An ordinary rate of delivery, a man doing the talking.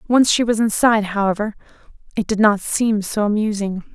No: average, 165 wpm; female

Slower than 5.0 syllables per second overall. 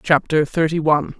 No: 5.6 syllables/s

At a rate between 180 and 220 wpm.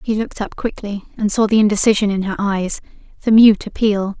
Yes: average, 200 wpm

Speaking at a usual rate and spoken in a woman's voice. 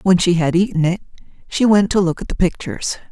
No: fast, 230 wpm; female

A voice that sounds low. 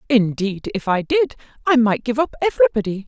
No: high, 235 Hz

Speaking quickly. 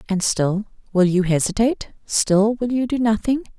No: average, 165 wpm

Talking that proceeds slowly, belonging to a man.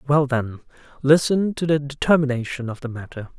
No: average, 160 wpm; male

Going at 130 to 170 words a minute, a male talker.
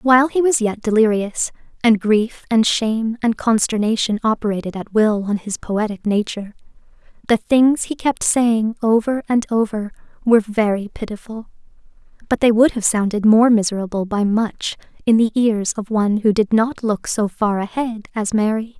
No: average, 165 wpm; female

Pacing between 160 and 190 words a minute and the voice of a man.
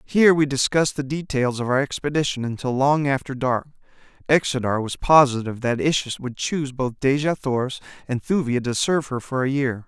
Yes: average, 180 wpm; male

